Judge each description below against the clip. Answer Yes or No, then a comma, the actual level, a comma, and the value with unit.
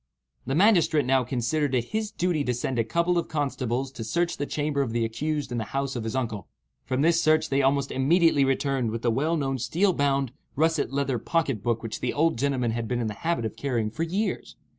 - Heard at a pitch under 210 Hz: Yes, low, 135 Hz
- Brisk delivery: Yes, fast, 225 wpm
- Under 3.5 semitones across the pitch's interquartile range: No, average, 4.6 semitones